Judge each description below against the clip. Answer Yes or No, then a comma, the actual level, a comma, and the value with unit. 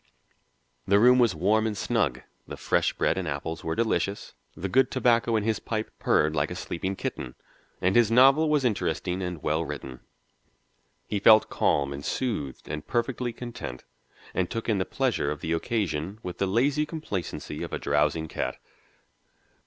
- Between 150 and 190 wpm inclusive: Yes, average, 170 wpm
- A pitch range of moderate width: No, wide, 6.8 semitones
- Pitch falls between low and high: No, low, 100 Hz